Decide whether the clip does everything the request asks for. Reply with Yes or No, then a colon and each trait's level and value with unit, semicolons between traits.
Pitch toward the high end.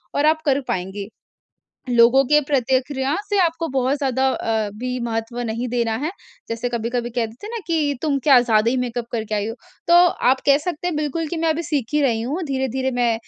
Yes: very high, 260 Hz